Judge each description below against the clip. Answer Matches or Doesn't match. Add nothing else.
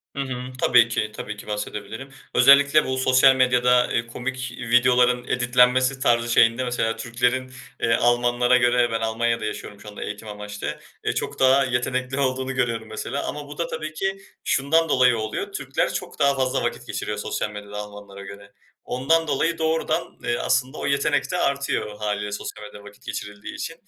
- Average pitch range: Matches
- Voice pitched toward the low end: Matches